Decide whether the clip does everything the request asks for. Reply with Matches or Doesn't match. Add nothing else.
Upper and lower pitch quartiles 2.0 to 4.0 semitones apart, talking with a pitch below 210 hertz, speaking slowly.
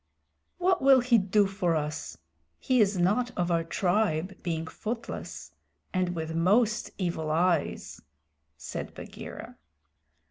Doesn't match